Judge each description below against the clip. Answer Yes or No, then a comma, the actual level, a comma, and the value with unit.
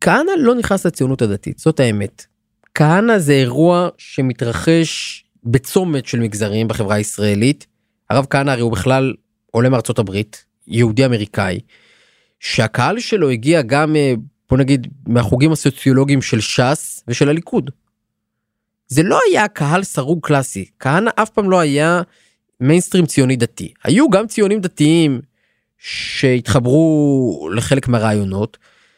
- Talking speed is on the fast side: No, average, 120 wpm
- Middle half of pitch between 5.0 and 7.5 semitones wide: Yes, wide, 5.6 semitones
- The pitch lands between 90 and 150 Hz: Yes, low, 135 Hz